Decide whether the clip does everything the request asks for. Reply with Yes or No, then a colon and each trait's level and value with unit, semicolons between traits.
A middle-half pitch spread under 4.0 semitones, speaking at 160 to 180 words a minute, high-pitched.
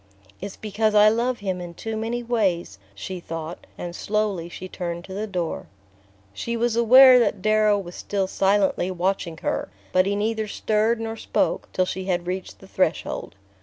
Yes: average, 3.5 semitones; average, 175 wpm; high, 200 Hz